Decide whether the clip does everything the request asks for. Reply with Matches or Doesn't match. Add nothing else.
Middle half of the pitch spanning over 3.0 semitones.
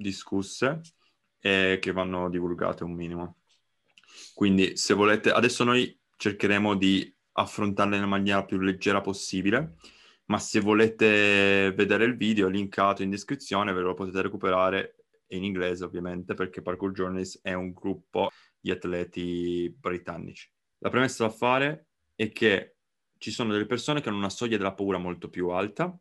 Doesn't match